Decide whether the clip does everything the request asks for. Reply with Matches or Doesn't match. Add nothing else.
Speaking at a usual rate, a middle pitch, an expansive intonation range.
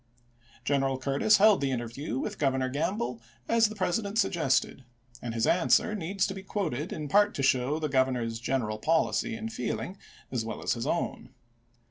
Matches